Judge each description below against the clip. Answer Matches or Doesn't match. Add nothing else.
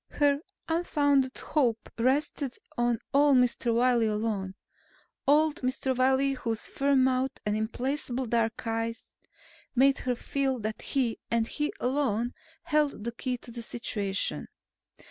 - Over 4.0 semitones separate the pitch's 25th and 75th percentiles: Doesn't match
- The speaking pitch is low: Doesn't match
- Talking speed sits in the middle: Doesn't match